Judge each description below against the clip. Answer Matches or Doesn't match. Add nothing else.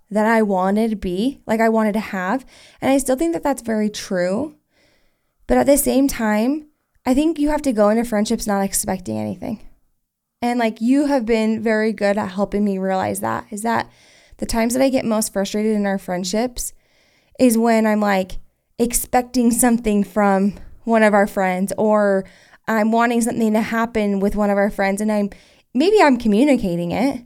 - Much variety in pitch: Doesn't match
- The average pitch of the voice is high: Matches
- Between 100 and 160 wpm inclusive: Doesn't match